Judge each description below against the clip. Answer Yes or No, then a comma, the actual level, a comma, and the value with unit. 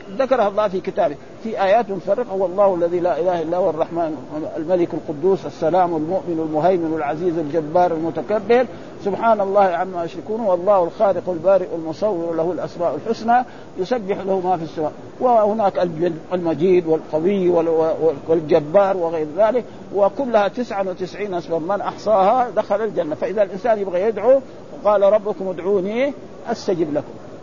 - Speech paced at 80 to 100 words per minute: No, average, 130 wpm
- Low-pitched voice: No, medium, 185 Hz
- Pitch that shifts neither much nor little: Yes, average, 3.8 semitones